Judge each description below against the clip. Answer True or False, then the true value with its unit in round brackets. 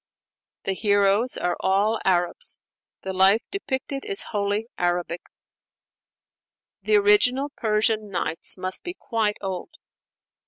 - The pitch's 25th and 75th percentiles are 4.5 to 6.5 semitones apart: True (5.1 semitones)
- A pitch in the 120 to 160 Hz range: False (210 Hz)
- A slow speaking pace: True (110 wpm)